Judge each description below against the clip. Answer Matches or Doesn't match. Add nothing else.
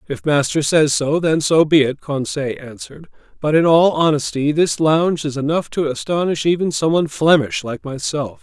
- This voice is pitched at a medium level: Matches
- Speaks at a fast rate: Doesn't match